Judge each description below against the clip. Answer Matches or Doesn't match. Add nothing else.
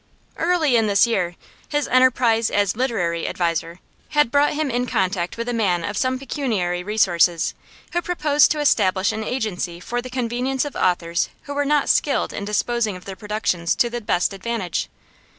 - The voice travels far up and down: Matches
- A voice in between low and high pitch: Doesn't match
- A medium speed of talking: Matches